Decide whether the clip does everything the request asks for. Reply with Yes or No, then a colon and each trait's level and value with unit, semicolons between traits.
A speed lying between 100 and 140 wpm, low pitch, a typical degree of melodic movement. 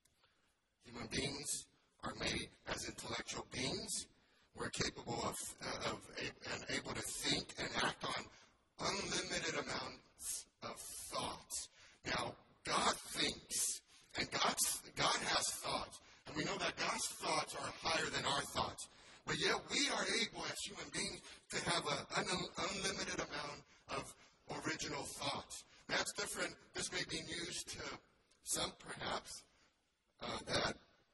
No: slow, 135 wpm; medium, 170 Hz; average, 3.9 semitones